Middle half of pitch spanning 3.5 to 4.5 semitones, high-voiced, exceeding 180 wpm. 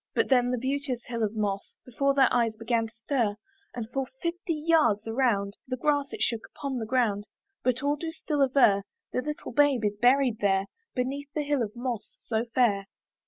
Yes: average, 3.9 semitones; very high, 250 Hz; average, 200 wpm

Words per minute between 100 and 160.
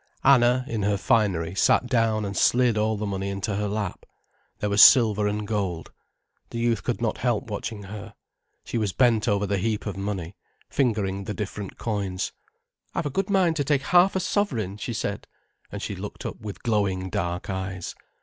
No: average, 190 wpm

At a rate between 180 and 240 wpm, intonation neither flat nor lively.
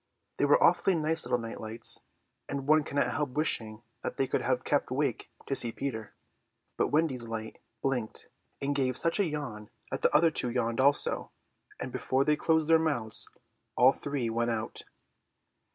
Yes: average, 185 wpm; average, 4.4 semitones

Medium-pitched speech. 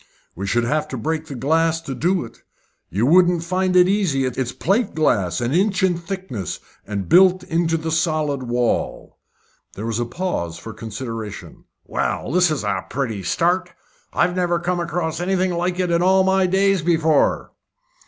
Yes: medium, 165 Hz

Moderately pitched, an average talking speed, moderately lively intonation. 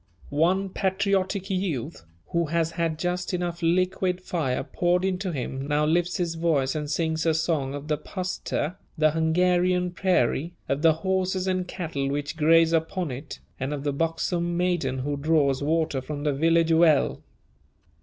Yes: medium, 165 Hz; average, 160 wpm; average, 3.3 semitones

